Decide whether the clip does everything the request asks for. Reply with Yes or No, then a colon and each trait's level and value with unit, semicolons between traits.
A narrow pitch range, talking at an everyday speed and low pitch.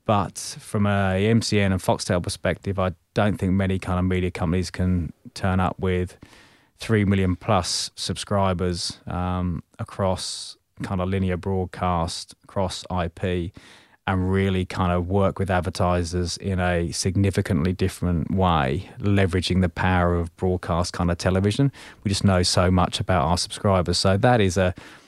Yes: narrow, 1.7 semitones; average, 150 wpm; very low, 95 Hz